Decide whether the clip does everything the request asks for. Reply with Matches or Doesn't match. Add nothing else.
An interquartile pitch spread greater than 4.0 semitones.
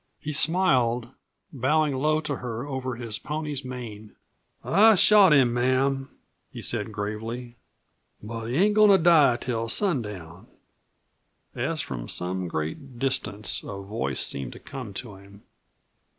Matches